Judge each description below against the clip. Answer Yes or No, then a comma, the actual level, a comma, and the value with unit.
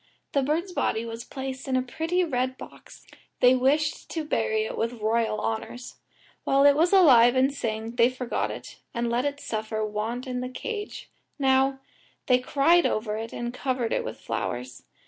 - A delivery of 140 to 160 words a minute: No, average, 180 wpm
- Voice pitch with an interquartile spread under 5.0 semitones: Yes, average, 3.6 semitones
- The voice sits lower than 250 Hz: No, very high, 255 Hz